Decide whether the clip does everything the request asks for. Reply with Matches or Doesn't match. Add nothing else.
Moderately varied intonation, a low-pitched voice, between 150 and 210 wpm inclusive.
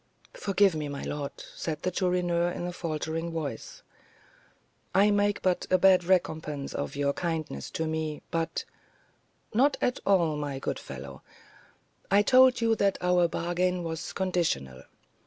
Doesn't match